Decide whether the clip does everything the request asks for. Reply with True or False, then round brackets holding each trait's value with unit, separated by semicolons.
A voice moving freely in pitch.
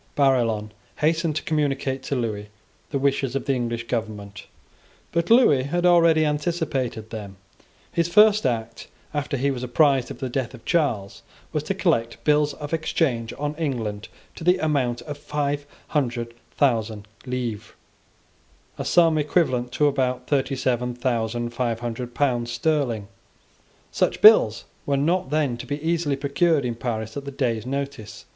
False (4.1 semitones)